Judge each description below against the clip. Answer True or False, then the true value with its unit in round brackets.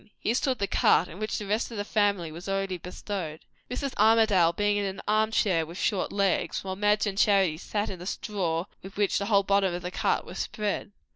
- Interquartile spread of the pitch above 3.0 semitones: False (2.4 semitones)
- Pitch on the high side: True (200 Hz)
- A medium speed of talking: False (225 wpm)